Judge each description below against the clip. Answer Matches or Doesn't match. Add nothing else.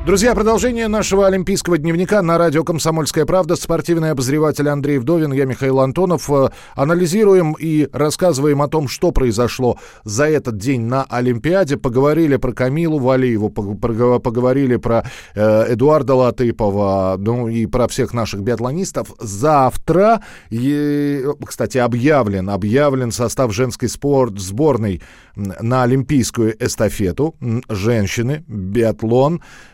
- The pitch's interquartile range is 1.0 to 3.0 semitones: Doesn't match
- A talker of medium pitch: Doesn't match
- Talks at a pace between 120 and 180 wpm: Doesn't match